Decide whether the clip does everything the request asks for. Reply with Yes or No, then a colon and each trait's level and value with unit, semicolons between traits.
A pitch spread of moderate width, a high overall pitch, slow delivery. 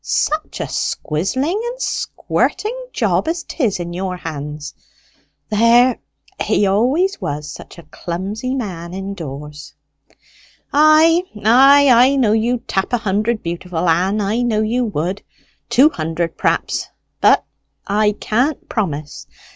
No: wide, 7.0 semitones; high, 210 Hz; slow, 125 wpm